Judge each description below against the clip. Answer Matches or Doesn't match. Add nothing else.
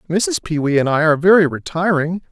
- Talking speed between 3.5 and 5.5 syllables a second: Doesn't match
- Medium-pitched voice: Matches